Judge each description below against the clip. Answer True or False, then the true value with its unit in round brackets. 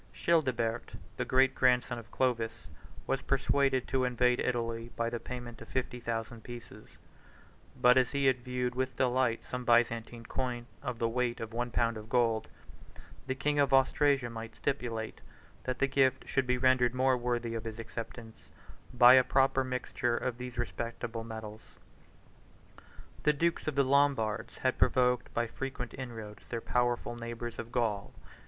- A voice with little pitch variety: True (2.0 semitones)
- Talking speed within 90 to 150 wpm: False (160 wpm)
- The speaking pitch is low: True (120 Hz)